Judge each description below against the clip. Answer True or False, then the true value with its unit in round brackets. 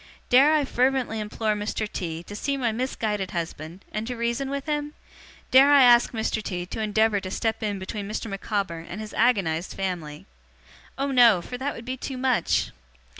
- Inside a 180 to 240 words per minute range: True (185 wpm)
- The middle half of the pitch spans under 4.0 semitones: False (4.6 semitones)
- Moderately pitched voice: False (220 Hz)